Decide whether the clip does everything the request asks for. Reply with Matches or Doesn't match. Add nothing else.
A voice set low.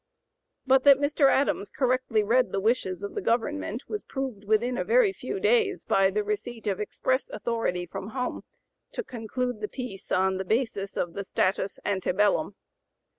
Doesn't match